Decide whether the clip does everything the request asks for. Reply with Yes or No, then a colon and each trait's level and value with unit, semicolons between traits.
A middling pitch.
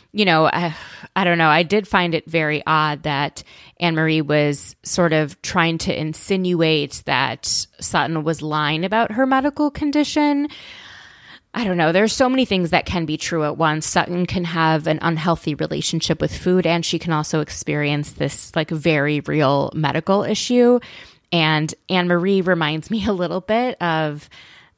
Yes: medium, 165 Hz